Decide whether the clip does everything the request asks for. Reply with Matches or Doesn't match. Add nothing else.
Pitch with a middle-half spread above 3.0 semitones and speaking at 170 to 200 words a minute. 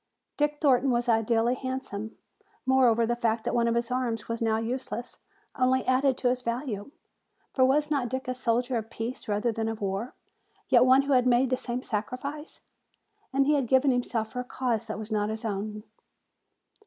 Doesn't match